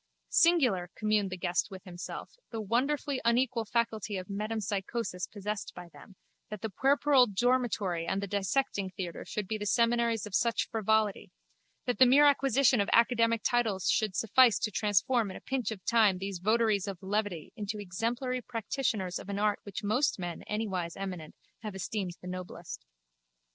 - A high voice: Yes, high, 210 Hz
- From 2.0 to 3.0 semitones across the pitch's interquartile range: No, average, 3.6 semitones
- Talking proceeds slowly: No, average, 165 wpm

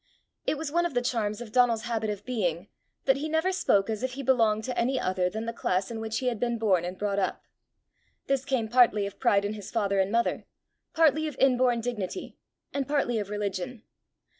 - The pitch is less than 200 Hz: No, high, 230 Hz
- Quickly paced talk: Yes, fast, 215 wpm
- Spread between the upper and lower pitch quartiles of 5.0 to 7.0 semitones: No, average, 4.0 semitones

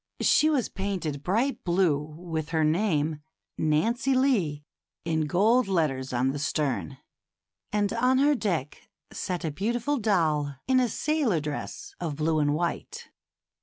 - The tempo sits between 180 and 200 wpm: No, average, 140 wpm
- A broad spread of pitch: Yes, wide, 7.2 semitones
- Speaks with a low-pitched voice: No, medium, 170 Hz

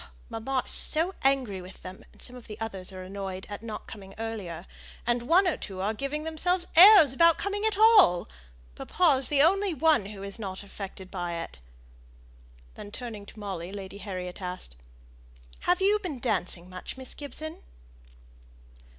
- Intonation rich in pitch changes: Yes, wide, 8.6 semitones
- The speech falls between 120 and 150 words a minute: No, average, 170 wpm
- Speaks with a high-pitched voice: Yes, high, 225 Hz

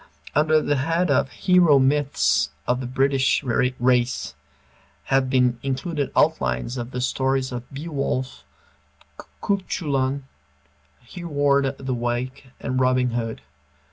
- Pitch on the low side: Yes, low, 130 Hz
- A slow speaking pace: Yes, slow, 110 wpm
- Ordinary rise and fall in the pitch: No, narrow, 2.3 semitones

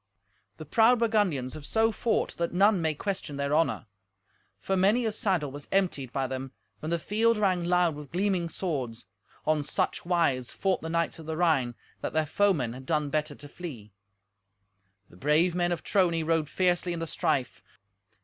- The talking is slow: No, average, 180 wpm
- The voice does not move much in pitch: No, average, 4.4 semitones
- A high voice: No, medium, 165 Hz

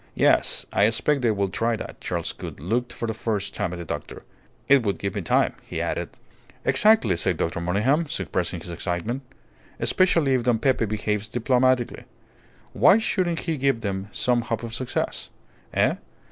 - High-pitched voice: No, low, 115 Hz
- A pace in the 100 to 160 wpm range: No, average, 175 wpm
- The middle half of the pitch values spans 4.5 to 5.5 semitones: Yes, average, 4.8 semitones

